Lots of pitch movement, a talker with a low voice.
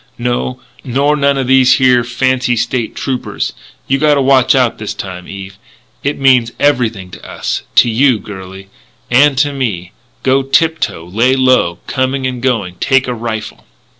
No: average, 3.5 semitones; low, 125 Hz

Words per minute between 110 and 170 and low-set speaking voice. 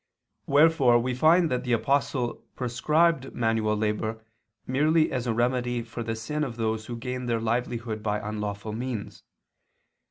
Yes: average, 150 wpm; low, 120 Hz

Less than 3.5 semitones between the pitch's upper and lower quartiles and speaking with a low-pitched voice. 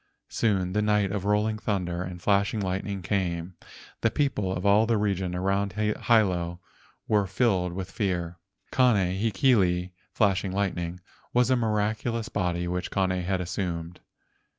Yes: average, 2.8 semitones; very low, 95 Hz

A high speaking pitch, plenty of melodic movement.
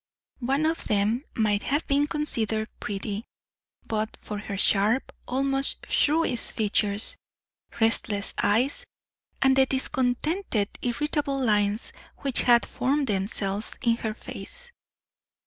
No: high, 235 Hz; average, 4.6 semitones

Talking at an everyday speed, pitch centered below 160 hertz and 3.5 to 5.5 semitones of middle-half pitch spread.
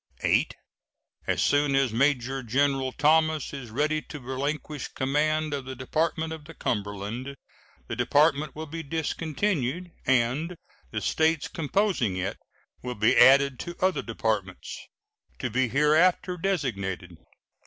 No: slow, 130 wpm; medium, 140 Hz; average, 3.9 semitones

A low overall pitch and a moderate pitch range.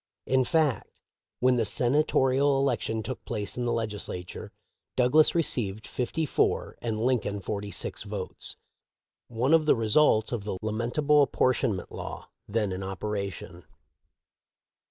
Yes: low, 115 Hz; average, 4.0 semitones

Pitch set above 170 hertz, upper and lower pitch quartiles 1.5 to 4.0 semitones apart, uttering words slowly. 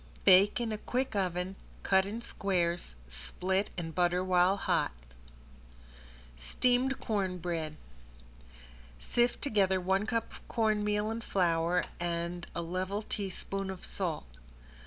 Yes: high, 190 Hz; average, 3.1 semitones; slow, 115 wpm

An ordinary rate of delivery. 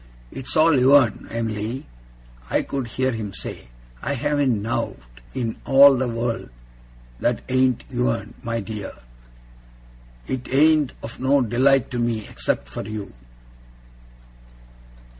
No: slow, 120 wpm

